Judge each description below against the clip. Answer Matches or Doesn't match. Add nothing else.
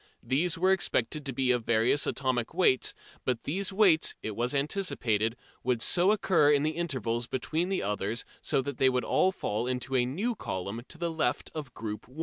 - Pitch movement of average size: Doesn't match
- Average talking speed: Matches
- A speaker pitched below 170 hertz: Matches